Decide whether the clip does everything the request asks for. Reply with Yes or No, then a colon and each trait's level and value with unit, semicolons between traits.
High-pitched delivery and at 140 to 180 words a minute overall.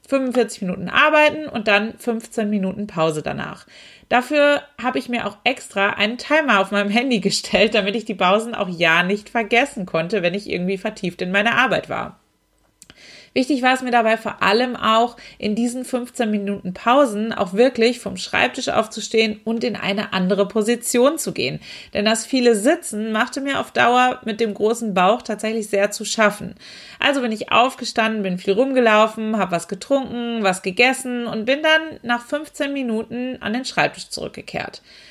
Yes: high, 225 Hz; average, 175 wpm